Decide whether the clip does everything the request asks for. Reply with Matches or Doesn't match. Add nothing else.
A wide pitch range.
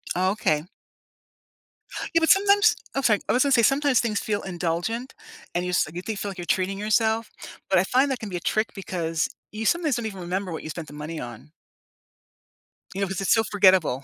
Doesn't match